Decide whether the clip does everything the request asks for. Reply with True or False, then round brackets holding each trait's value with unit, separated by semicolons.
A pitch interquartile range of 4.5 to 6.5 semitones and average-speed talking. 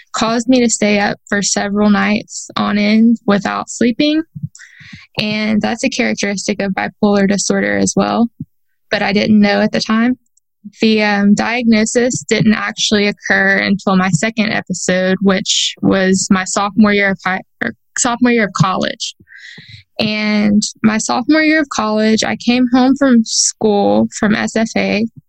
False (2.4 semitones; 150 wpm)